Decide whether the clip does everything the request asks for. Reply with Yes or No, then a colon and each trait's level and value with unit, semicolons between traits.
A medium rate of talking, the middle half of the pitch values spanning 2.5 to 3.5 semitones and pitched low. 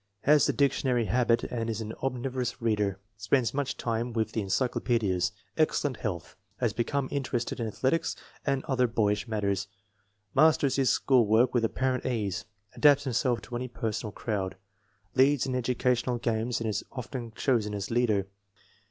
Yes: average, 160 wpm; average, 3.1 semitones; low, 120 Hz